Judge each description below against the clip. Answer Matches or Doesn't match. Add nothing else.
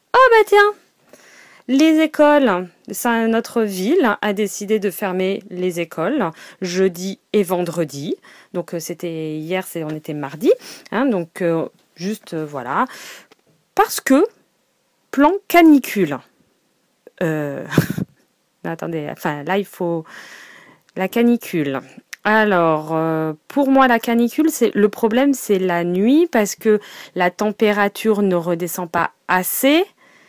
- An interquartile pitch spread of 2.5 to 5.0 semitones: Doesn't match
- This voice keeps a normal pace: Doesn't match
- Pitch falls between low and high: Doesn't match